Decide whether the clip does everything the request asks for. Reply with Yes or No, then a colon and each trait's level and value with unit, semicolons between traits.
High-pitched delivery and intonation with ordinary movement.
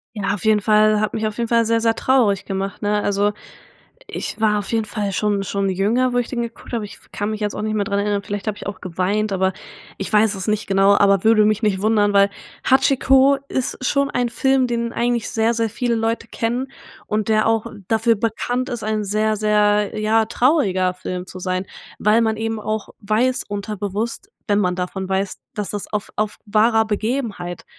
No: high, 215 Hz; narrow, 2.2 semitones